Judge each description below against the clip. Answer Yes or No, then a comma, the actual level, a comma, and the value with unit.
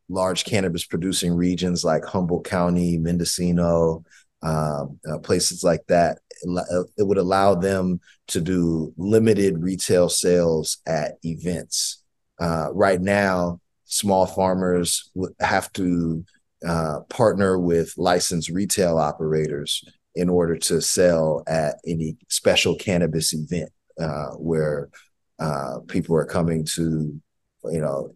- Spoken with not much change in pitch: Yes, narrow, 2.1 semitones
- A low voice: Yes, very low, 85 Hz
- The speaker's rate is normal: No, slow, 115 wpm